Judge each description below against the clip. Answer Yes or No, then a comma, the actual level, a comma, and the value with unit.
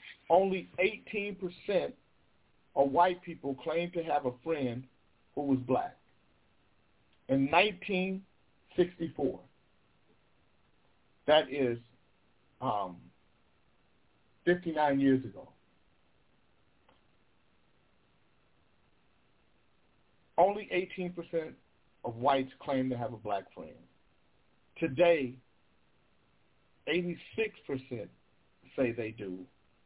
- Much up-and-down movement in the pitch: Yes, wide, 6.0 semitones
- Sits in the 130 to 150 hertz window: Yes, medium, 140 Hz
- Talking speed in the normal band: No, slow, 80 wpm